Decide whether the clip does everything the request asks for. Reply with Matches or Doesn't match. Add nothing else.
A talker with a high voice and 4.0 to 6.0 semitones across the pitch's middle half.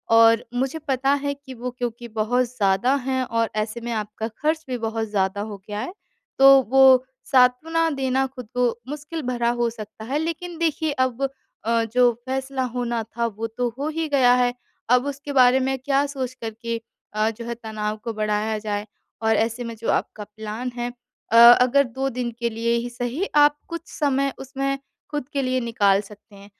Doesn't match